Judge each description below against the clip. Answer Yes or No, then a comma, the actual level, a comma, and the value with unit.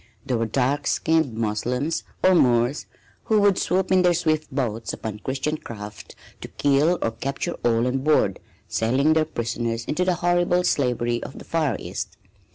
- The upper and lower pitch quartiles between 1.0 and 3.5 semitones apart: No, wide, 5.6 semitones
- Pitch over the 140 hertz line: No, low, 135 Hz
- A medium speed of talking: Yes, average, 165 wpm